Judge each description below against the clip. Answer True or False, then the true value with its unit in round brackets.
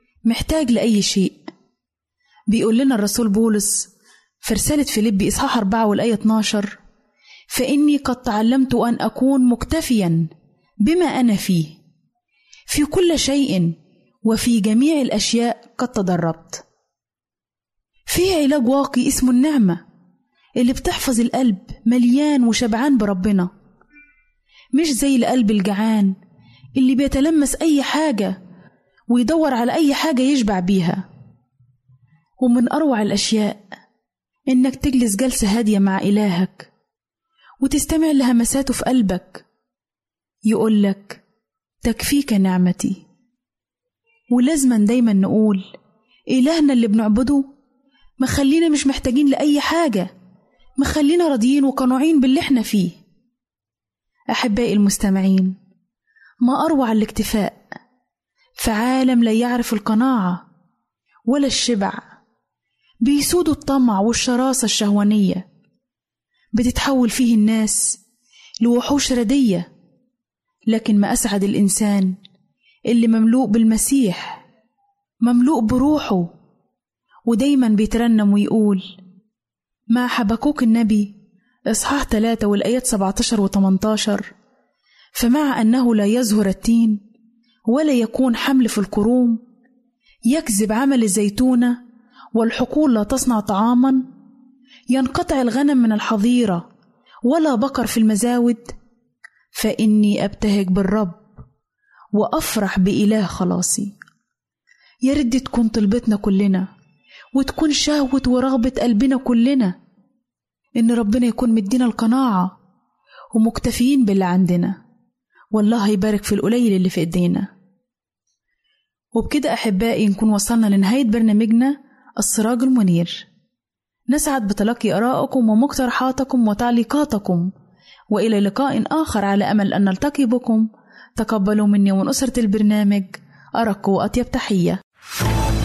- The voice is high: True (230 Hz)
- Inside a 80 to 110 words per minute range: True (95 wpm)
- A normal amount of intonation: True (4.0 semitones)